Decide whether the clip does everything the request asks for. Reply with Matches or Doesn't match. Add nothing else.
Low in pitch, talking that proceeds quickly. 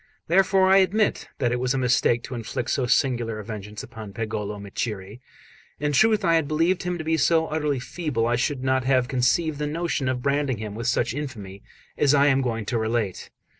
Matches